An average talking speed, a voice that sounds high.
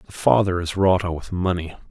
No: average, 190 wpm; very low, 90 Hz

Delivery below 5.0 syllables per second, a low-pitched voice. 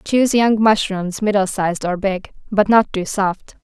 No: 4.5 syllables/s; high, 200 Hz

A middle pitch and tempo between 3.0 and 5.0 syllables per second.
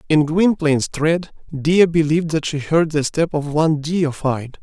Yes: medium, 155 Hz; 4.5 syllables/s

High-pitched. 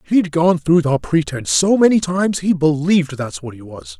No: medium, 155 Hz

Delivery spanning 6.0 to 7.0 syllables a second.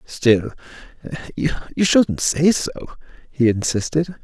No: 3.8 syllables/s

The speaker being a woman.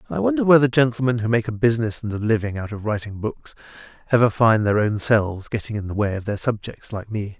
No: male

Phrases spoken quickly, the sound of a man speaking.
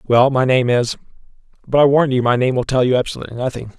Yes: fast, 220 wpm; male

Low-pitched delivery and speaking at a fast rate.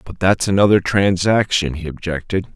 No: very low, 90 Hz; average, 140 wpm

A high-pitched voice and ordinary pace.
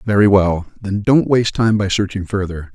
No: low, 100 Hz; average, 195 wpm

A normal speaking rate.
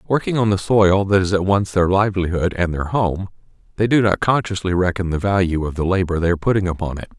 No: fast, 235 wpm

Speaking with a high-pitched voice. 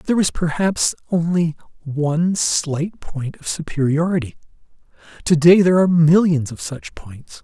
No: medium, 160 Hz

